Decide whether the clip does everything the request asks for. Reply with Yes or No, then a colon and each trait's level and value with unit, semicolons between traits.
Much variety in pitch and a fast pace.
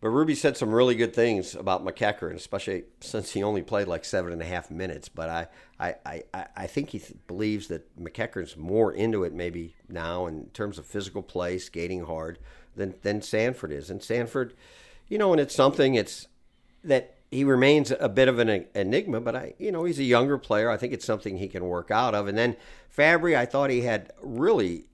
Yes: wide, 5.9 semitones; fast, 215 wpm